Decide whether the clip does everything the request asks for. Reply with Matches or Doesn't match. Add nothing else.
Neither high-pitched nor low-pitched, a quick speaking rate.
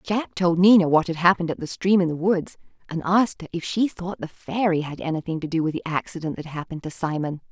Matches